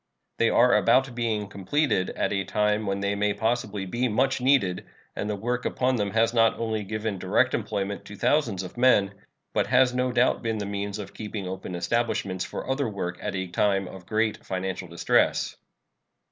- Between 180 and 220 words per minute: Yes, average, 190 wpm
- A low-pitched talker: Yes, low, 105 Hz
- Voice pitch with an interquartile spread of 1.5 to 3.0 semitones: No, average, 3.4 semitones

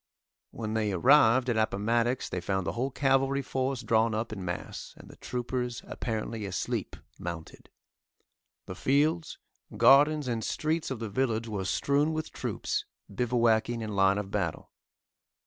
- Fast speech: No, average, 145 wpm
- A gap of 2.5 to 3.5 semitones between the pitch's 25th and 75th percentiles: No, average, 3.9 semitones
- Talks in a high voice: No, low, 115 Hz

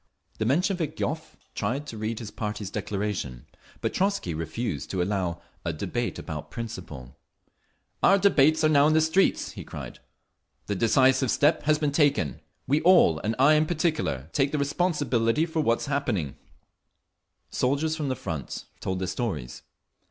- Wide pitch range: Yes, wide, 8.4 semitones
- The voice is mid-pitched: No, low, 125 Hz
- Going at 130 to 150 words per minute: No, average, 165 wpm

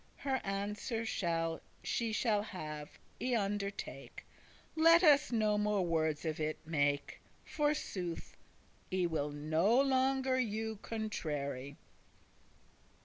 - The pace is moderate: No, slow, 100 wpm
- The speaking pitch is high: Yes, high, 205 Hz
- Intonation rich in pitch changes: Yes, wide, 7.3 semitones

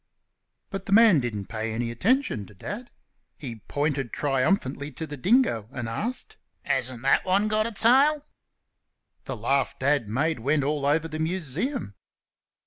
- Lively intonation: Yes, wide, 8.5 semitones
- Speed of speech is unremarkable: Yes, average, 150 wpm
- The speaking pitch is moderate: Yes, medium, 145 Hz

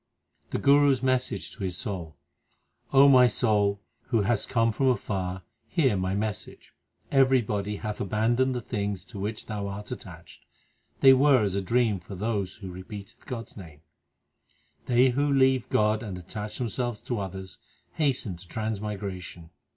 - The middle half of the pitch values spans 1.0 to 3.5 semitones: No, average, 4.3 semitones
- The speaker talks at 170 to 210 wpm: No, average, 160 wpm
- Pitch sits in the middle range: No, low, 105 Hz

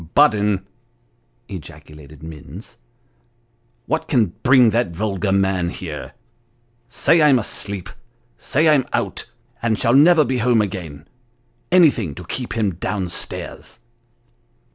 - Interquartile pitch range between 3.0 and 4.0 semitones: No, average, 4.9 semitones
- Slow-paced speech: Yes, slow, 130 wpm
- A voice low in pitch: Yes, low, 110 Hz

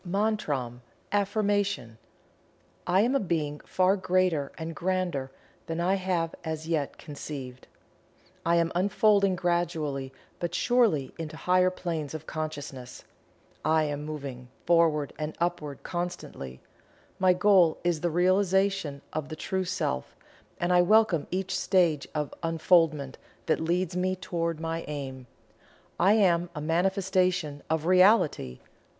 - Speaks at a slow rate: Yes, slow, 130 wpm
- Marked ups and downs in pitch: No, average, 3.6 semitones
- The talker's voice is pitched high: No, medium, 170 Hz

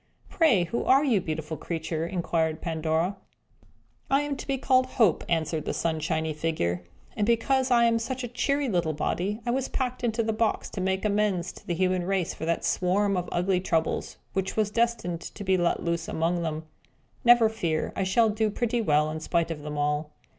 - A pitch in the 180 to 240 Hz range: Yes, medium, 185 Hz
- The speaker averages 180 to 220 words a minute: Yes, average, 195 wpm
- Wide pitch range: Yes, wide, 6.0 semitones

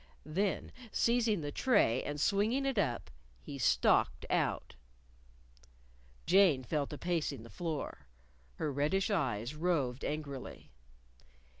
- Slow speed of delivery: Yes, slow, 120 wpm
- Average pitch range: No, wide, 6.2 semitones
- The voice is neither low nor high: Yes, medium, 155 Hz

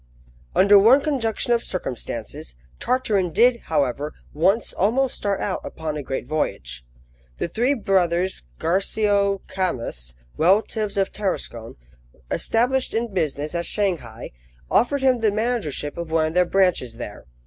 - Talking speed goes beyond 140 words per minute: No, slow, 135 wpm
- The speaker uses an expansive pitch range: Yes, wide, 6.6 semitones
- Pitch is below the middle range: No, high, 190 Hz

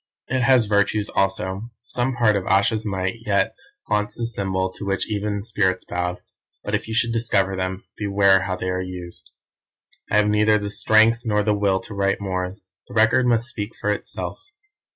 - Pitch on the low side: Yes, low, 105 Hz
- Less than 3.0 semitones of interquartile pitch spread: Yes, narrow, 2.5 semitones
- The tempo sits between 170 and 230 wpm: Yes, average, 185 wpm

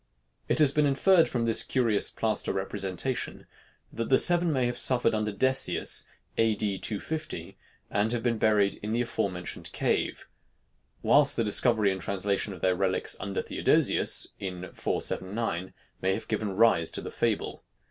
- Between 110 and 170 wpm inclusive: Yes, average, 160 wpm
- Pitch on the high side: No, low, 110 Hz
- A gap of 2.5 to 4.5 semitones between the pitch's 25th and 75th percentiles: Yes, average, 3.8 semitones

